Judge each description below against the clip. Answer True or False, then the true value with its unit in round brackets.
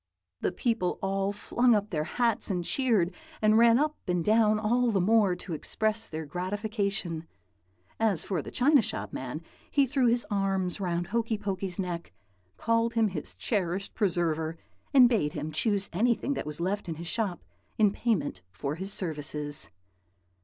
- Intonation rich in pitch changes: False (4.7 semitones)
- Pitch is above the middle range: True (200 Hz)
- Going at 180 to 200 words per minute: False (165 wpm)